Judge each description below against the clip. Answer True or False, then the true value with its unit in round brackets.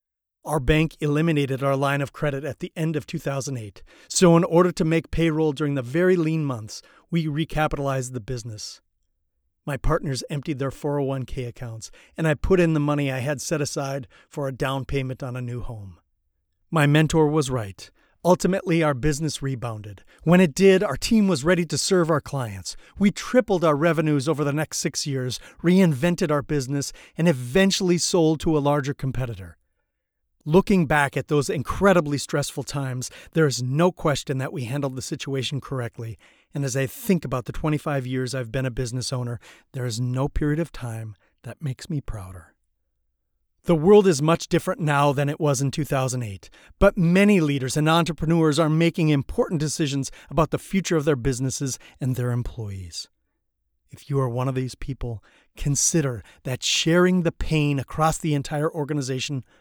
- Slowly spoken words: False (175 wpm)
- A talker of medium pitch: True (145 Hz)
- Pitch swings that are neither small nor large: True (4.2 semitones)